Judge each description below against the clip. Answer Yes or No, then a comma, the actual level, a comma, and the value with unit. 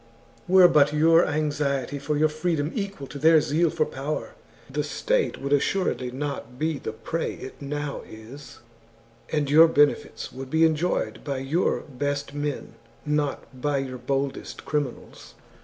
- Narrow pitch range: Yes, narrow, 2.3 semitones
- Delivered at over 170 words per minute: No, average, 150 wpm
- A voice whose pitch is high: No, medium, 145 Hz